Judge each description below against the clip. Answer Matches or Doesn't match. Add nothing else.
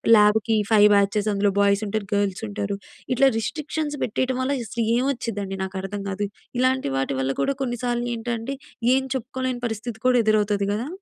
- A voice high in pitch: Matches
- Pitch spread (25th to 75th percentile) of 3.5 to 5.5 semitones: Matches